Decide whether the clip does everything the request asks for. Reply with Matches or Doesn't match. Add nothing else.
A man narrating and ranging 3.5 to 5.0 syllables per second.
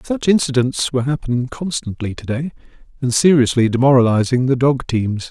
Doesn't match